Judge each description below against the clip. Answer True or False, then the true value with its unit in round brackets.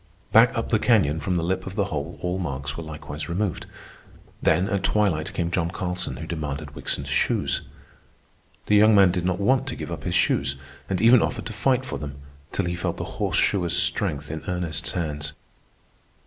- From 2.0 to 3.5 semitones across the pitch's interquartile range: False (4.3 semitones)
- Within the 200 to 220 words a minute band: False (190 wpm)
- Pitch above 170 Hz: False (85 Hz)